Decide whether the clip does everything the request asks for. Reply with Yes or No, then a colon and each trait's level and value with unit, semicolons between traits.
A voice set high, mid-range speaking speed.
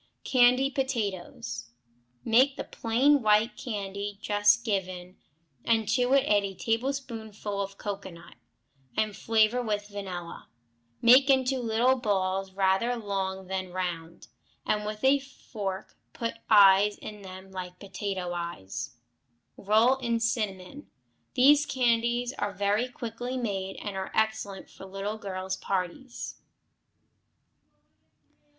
No: high, 210 Hz; slow, 120 wpm